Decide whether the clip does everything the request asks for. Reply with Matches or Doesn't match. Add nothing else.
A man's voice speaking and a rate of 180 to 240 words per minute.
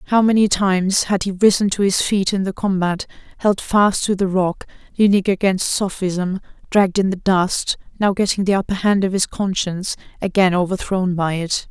Doesn't match